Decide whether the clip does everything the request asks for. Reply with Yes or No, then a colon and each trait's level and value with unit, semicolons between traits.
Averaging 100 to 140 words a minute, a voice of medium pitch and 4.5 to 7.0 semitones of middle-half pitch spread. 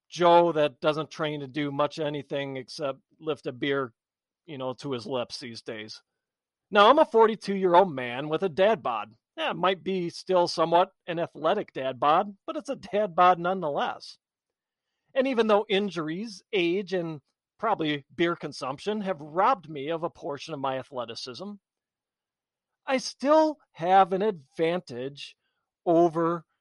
No: average, 160 wpm; medium, 170 Hz; average, 5.2 semitones